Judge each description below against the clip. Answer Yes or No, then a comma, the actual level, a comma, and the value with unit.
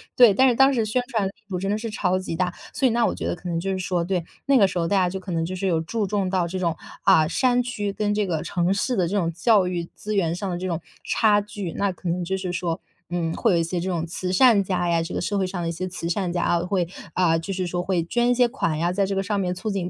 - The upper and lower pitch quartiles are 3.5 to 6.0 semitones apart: No, average, 2.9 semitones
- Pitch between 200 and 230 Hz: No, medium, 185 Hz